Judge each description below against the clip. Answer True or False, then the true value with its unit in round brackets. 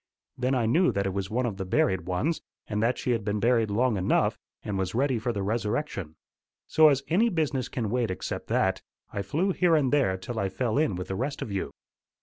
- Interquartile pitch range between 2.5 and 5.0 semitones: False (5.5 semitones)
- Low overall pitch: True (115 Hz)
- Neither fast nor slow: False (230 wpm)